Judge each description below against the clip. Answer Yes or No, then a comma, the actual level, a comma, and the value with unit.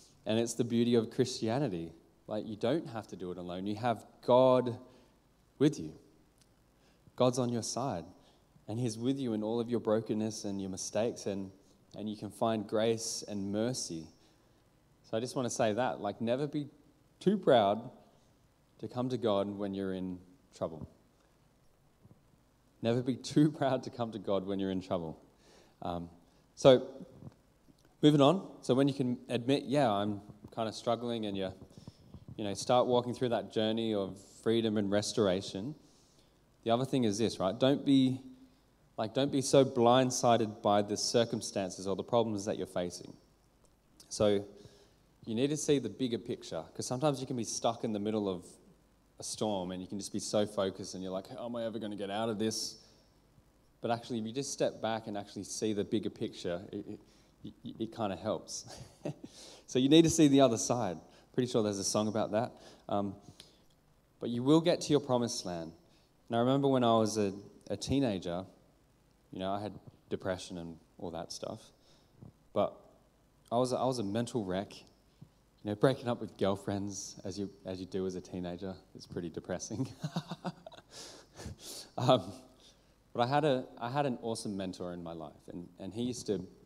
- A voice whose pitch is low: Yes, low, 110 Hz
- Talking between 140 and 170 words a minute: No, average, 185 wpm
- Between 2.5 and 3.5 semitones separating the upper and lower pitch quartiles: No, average, 4.1 semitones